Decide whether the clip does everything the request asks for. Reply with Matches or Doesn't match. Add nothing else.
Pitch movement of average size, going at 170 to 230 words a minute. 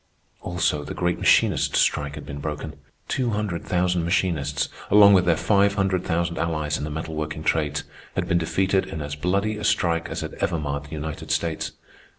Matches